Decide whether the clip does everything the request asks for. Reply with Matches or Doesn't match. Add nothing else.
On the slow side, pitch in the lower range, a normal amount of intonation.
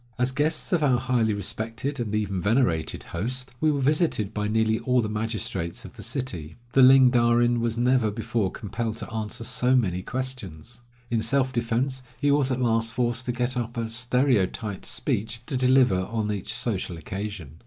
Doesn't match